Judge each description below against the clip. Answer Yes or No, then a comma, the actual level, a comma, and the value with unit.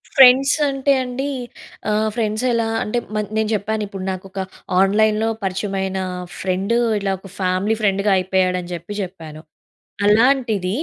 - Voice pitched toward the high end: Yes, high, 205 Hz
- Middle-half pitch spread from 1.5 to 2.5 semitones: No, average, 2.9 semitones